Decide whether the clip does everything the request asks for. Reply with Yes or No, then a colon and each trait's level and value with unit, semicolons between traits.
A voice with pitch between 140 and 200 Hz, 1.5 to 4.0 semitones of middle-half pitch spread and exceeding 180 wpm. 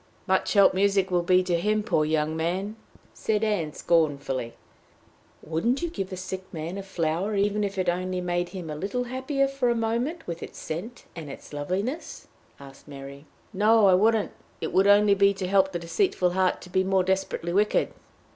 Yes: high, 190 Hz; average, 3.6 semitones; average, 190 wpm